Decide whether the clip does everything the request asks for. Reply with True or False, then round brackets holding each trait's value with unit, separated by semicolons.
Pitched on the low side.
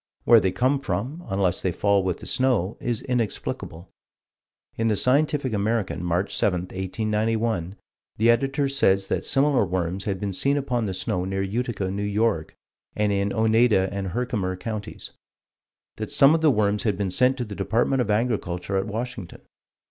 True (105 Hz)